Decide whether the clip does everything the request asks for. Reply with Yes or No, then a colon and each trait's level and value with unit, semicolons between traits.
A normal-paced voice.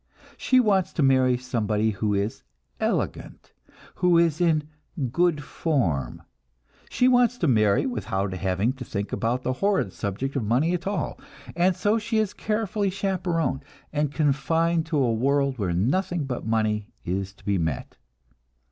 Yes: average, 155 wpm